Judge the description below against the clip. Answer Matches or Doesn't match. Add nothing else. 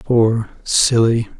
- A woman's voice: Doesn't match